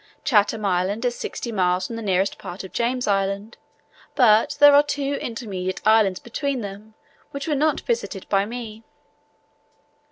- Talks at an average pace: Yes, average, 155 wpm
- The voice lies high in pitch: Yes, high, 220 Hz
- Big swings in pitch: No, average, 4.4 semitones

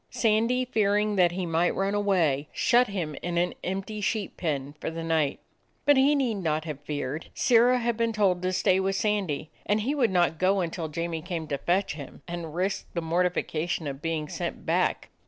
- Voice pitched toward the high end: No, medium, 180 Hz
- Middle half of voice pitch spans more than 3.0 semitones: Yes, average, 4.5 semitones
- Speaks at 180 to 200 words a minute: Yes, average, 195 wpm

